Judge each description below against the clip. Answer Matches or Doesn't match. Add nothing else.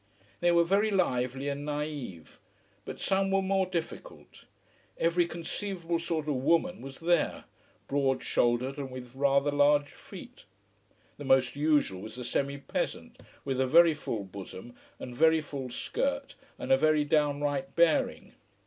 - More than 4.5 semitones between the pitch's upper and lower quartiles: Doesn't match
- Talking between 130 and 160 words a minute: Matches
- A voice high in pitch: Doesn't match